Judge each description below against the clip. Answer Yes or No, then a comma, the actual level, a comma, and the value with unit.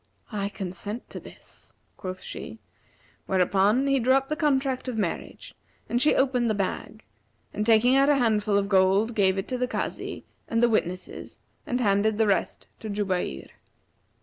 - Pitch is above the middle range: Yes, high, 215 Hz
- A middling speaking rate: Yes, average, 170 wpm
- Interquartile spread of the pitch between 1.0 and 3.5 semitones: No, average, 4.3 semitones